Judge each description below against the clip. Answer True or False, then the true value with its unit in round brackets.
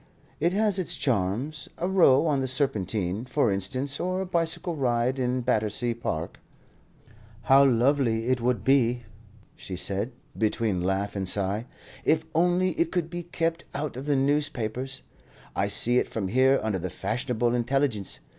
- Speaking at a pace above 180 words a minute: False (155 wpm)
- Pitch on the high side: False (125 Hz)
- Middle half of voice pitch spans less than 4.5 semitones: False (5.1 semitones)